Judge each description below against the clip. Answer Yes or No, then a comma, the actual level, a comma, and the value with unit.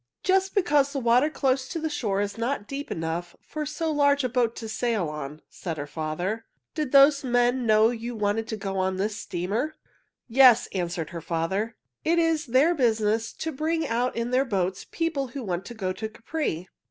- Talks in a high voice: Yes, high, 235 Hz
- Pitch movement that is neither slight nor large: No, wide, 6.4 semitones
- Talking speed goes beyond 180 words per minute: Yes, average, 195 wpm